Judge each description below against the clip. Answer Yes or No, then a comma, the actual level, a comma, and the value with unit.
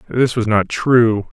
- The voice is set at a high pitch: No, low, 115 Hz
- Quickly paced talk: No, average, 175 wpm